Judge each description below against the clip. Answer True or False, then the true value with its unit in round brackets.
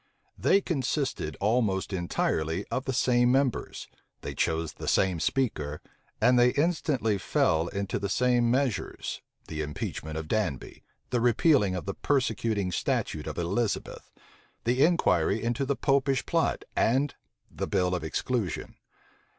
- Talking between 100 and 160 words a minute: True (135 wpm)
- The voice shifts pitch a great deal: True (6.3 semitones)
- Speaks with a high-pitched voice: False (115 Hz)